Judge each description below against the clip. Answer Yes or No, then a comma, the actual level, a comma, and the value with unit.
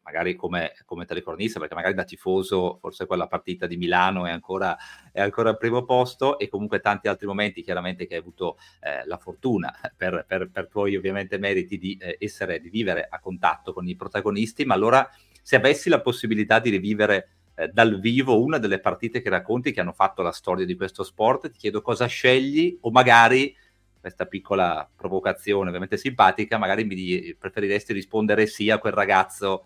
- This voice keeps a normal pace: No, fast, 180 wpm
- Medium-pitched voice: No, low, 105 Hz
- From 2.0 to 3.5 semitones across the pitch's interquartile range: Yes, average, 3.1 semitones